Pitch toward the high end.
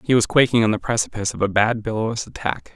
No: low, 115 Hz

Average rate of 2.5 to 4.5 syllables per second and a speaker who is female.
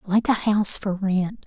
Yes: 4.4 syllables/s; female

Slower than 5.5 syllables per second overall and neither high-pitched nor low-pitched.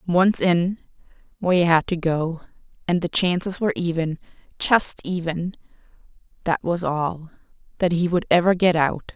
Yes: 4.8 syllables/s; medium, 175 Hz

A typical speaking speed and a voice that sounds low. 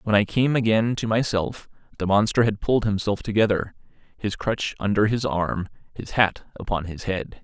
Yes: average, 175 wpm; low, 105 Hz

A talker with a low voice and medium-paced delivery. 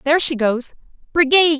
No: very high, 290 Hz; average, 150 wpm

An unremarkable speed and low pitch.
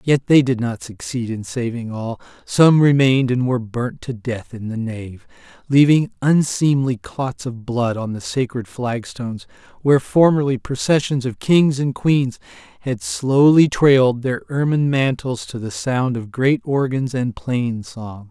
Yes: average, 160 wpm; low, 125 Hz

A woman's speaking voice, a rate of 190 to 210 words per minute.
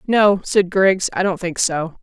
Yes: female; fast, 205 wpm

